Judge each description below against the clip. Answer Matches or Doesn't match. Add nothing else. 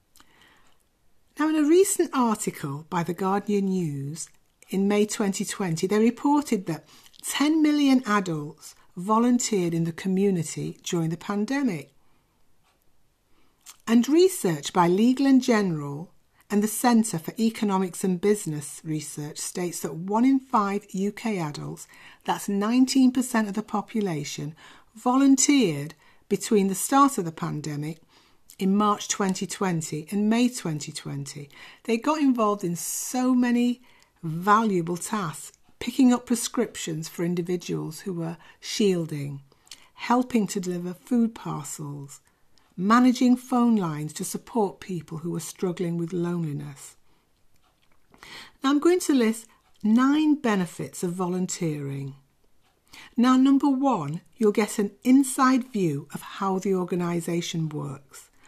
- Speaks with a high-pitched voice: Matches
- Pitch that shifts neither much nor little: Doesn't match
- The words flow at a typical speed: Doesn't match